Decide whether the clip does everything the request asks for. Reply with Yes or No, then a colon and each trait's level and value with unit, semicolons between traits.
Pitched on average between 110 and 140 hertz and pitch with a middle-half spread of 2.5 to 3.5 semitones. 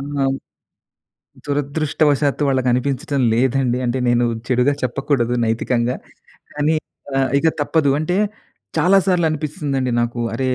Yes: low, 135 Hz; average, 3.0 semitones